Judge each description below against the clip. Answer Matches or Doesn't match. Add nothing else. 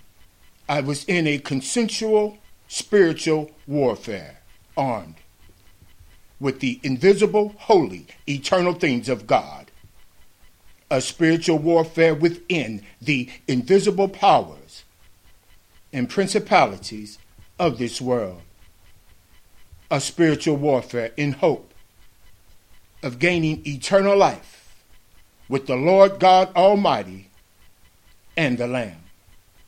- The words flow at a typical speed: Doesn't match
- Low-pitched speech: Matches